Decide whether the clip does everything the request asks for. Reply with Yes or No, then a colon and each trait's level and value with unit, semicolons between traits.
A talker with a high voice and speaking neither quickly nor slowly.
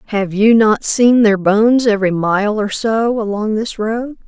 Yes: high, 215 Hz; average, 180 wpm